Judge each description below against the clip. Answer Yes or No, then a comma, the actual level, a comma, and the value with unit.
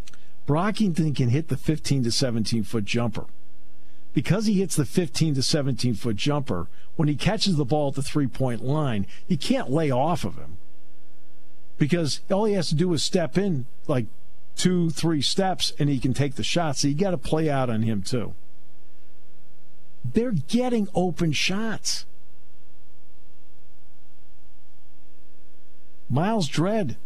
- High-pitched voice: No, low, 130 Hz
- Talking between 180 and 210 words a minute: No, average, 150 wpm